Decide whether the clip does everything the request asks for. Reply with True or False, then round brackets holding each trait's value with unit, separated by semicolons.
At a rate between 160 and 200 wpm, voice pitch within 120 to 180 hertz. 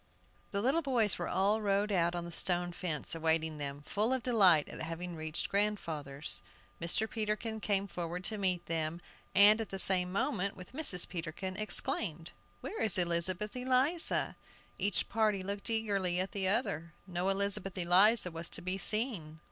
False (165 wpm; 190 Hz)